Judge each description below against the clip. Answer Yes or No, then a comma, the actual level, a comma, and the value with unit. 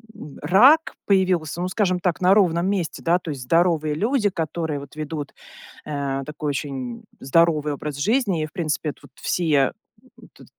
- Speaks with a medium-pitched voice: Yes, medium, 165 Hz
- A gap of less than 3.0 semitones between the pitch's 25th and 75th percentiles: No, average, 3.8 semitones